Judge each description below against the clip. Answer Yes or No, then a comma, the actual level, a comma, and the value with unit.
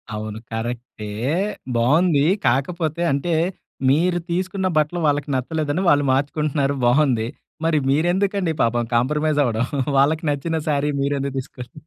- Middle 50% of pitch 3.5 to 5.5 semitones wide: Yes, average, 4.1 semitones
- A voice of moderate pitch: Yes, medium, 145 Hz